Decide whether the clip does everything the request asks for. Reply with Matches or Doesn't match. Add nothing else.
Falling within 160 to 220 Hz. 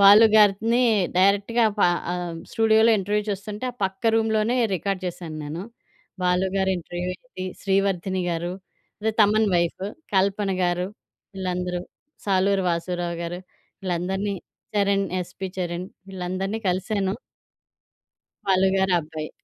Matches